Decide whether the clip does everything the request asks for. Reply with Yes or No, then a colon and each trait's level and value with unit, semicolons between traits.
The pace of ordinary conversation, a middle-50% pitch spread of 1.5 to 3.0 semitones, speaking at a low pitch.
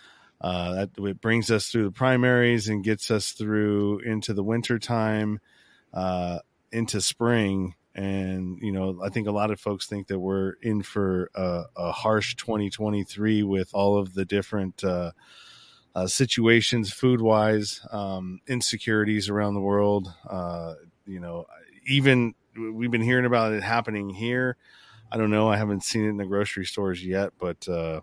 Yes: average, 165 wpm; average, 2.7 semitones; low, 105 Hz